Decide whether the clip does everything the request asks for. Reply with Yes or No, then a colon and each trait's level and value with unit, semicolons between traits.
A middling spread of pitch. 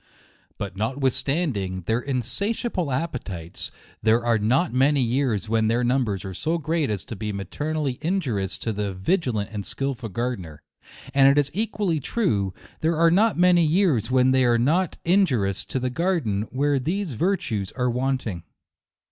No: wide, 6.8 semitones